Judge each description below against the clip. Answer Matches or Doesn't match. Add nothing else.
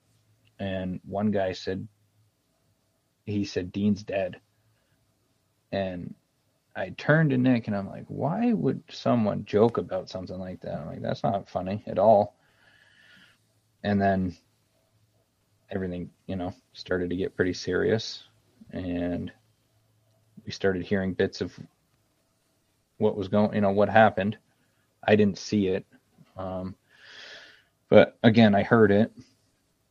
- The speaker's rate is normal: Doesn't match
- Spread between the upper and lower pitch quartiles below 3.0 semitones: Matches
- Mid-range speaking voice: Doesn't match